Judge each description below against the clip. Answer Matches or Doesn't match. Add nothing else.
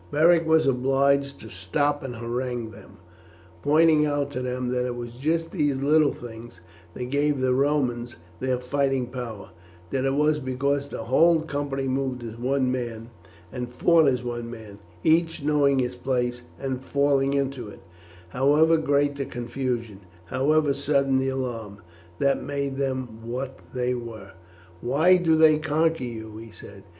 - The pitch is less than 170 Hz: Matches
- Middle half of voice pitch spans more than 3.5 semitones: Doesn't match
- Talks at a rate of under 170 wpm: Matches